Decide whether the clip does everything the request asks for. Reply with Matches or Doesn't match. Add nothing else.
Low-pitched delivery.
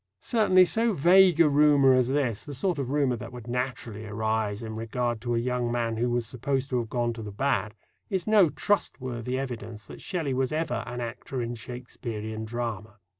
Matches